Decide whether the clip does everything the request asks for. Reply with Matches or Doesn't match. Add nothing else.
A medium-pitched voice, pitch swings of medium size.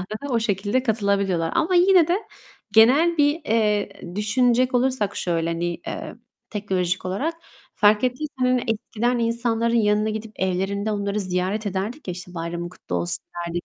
Doesn't match